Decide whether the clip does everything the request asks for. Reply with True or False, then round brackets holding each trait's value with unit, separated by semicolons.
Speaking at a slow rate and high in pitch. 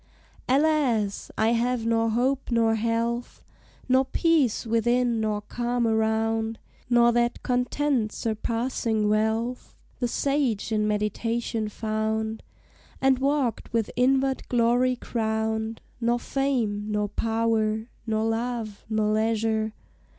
True (110 wpm; 230 Hz)